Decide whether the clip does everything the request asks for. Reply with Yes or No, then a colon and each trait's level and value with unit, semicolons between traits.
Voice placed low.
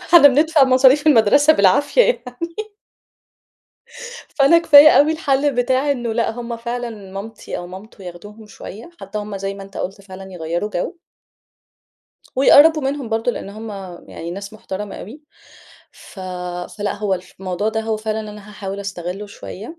No: high, 220 Hz